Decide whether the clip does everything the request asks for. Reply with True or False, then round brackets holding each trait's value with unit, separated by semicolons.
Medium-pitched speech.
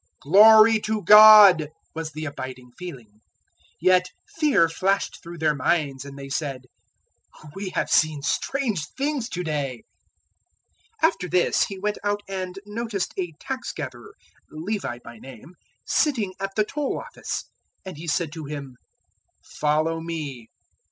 True (175 Hz)